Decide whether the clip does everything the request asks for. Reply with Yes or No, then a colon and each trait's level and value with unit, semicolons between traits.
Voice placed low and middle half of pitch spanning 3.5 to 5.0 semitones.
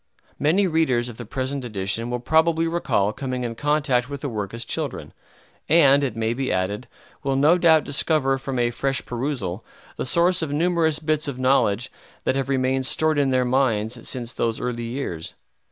Yes: low, 130 Hz; average, 3.9 semitones